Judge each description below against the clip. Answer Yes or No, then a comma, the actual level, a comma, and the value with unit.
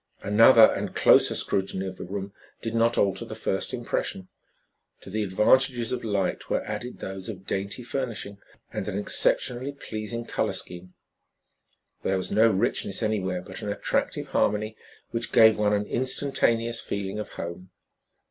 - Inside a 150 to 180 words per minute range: Yes, average, 155 wpm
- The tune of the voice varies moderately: Yes, average, 3.2 semitones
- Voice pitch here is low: Yes, low, 105 Hz